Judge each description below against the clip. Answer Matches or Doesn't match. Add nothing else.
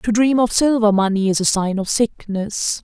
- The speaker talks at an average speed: Doesn't match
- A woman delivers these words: Matches